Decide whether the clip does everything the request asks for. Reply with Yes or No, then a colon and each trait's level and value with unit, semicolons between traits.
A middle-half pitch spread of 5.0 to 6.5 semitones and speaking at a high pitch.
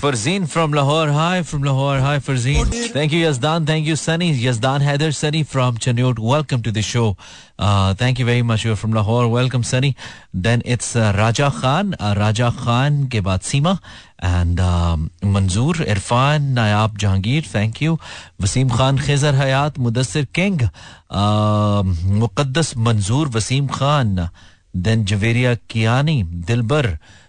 No: average, 5.3 semitones; low, 120 Hz